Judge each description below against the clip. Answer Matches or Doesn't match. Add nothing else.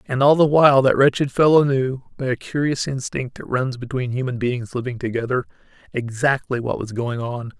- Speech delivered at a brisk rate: Doesn't match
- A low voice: Matches